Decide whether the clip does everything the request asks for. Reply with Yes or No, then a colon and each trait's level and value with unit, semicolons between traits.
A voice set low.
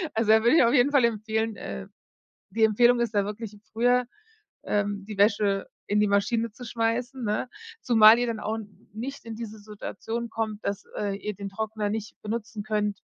No: high, 220 Hz